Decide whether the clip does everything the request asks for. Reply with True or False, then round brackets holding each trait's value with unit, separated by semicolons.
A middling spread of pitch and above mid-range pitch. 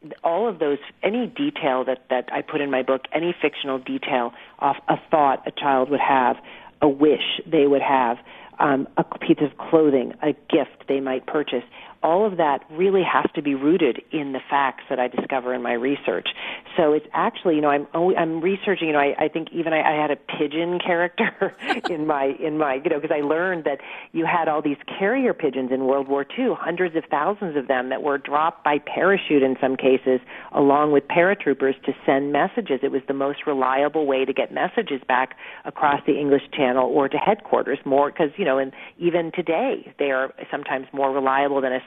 False (3.4 semitones; 145 Hz)